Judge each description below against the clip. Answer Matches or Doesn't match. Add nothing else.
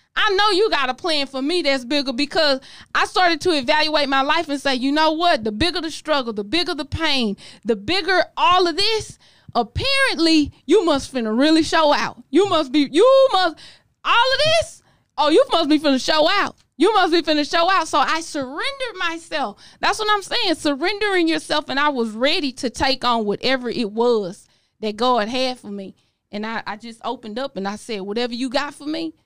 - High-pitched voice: Matches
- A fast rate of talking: Matches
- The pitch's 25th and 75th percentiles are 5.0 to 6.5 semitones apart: Matches